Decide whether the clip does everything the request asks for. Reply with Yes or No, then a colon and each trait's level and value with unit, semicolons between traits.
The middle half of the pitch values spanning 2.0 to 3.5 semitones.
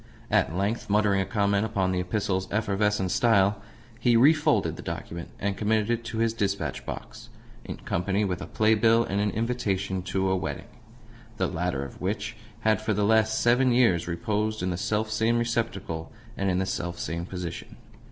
Yes: average, 3.1 semitones